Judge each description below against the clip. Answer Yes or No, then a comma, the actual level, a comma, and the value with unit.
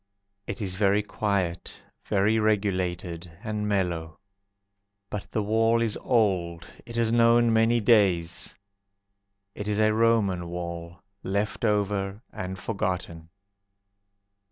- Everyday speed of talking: No, slow, 110 wpm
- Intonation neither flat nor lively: Yes, average, 3.6 semitones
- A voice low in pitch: Yes, low, 100 Hz